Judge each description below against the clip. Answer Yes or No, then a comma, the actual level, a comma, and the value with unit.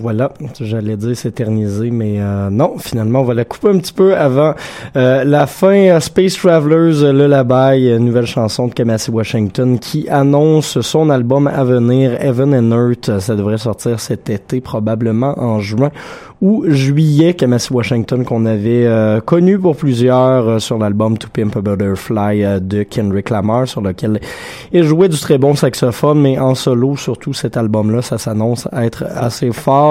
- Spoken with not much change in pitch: No, average, 4.2 semitones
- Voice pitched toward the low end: Yes, low, 125 Hz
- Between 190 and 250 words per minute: No, average, 170 wpm